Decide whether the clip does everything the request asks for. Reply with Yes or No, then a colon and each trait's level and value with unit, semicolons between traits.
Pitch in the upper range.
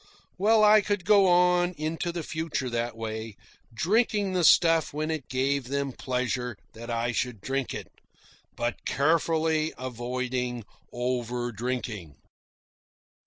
No: low, 130 Hz